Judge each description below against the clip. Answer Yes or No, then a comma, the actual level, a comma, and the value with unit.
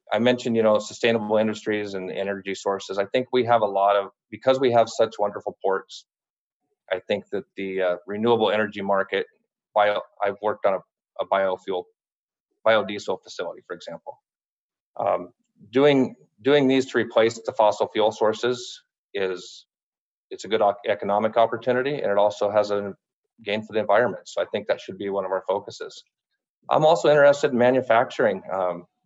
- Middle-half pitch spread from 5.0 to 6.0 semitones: No, average, 4.2 semitones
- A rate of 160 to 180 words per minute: Yes, average, 170 wpm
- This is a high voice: No, low, 115 Hz